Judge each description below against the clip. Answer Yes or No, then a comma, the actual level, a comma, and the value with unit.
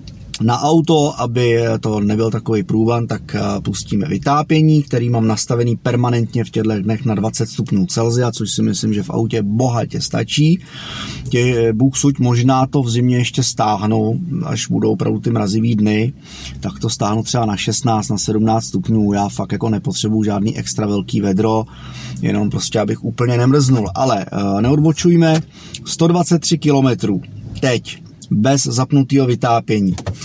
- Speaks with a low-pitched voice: Yes, low, 115 Hz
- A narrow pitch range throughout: No, average, 3.7 semitones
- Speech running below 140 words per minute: No, average, 145 wpm